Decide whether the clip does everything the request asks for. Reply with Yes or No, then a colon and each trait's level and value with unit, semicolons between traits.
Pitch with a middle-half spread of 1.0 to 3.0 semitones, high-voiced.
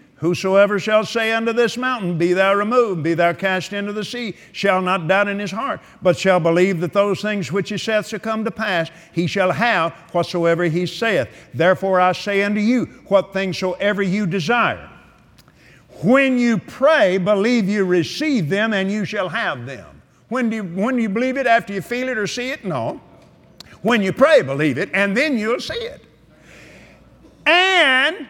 No: average, 3.9 semitones; high, 205 Hz